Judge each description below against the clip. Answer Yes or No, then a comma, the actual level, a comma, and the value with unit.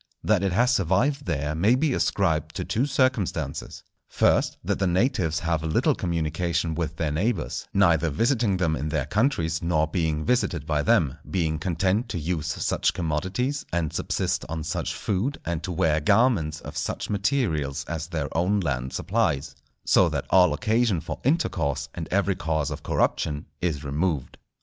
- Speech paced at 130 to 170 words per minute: Yes, average, 165 wpm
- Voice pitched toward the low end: Yes, very low, 85 Hz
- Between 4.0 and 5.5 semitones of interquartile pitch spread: Yes, average, 4.7 semitones